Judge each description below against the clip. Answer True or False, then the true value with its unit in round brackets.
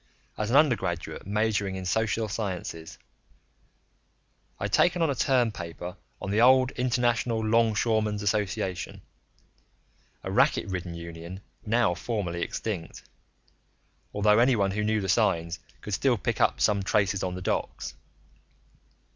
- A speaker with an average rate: False (130 wpm)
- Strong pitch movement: False (3.8 semitones)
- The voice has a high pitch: False (105 Hz)